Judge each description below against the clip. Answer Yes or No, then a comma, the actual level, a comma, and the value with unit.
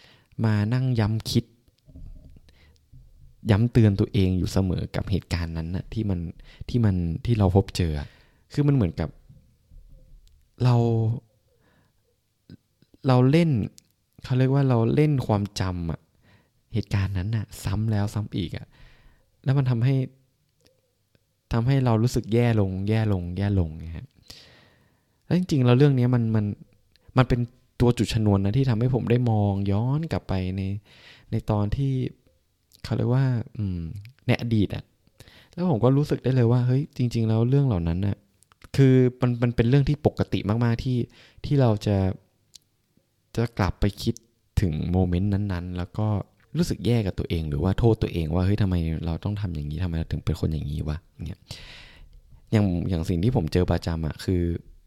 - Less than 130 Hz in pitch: Yes, low, 105 Hz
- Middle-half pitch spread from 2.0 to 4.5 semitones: No, average, 4.9 semitones